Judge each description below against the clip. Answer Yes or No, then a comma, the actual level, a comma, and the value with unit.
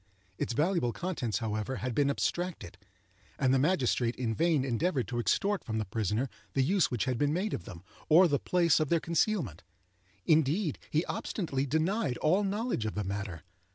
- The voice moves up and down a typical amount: No, wide, 6.6 semitones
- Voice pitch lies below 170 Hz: Yes, medium, 140 Hz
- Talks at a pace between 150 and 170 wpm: No, average, 180 wpm